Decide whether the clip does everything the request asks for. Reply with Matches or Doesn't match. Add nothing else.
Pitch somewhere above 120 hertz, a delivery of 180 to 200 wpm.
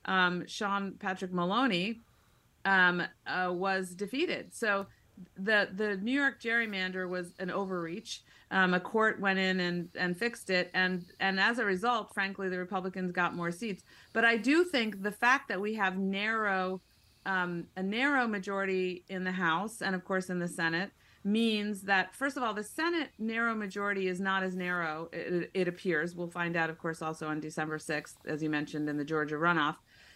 Matches